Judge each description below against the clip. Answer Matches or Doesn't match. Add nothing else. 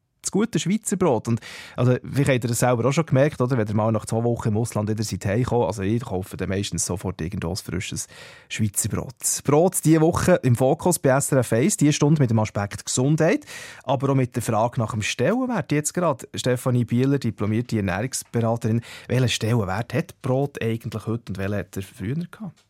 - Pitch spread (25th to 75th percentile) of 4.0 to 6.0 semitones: Matches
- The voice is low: Matches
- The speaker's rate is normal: Doesn't match